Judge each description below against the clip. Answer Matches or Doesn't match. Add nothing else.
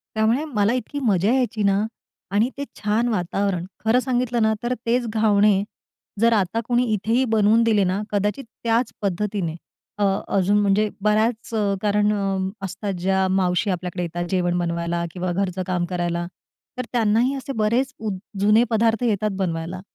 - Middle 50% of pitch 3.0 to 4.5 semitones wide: Matches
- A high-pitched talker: Matches